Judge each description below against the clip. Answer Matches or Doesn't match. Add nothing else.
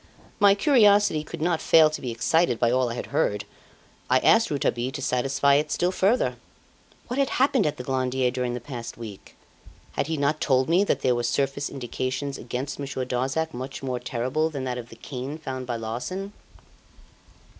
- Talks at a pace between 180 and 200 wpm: Matches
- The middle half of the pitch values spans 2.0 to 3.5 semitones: Doesn't match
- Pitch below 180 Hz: Matches